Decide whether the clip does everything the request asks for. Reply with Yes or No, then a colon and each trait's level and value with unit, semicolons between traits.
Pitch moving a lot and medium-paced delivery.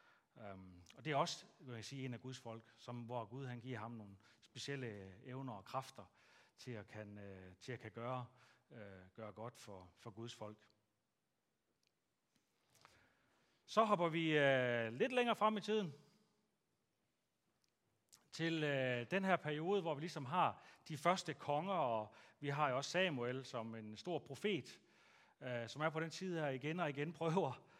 Yes: wide, 5.7 semitones; average, 175 wpm